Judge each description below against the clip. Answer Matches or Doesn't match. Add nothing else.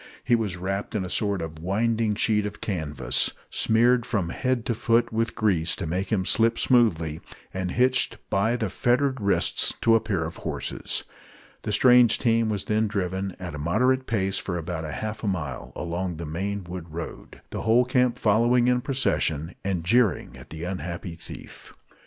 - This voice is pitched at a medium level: Doesn't match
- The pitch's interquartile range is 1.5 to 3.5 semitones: Doesn't match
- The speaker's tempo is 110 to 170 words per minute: Doesn't match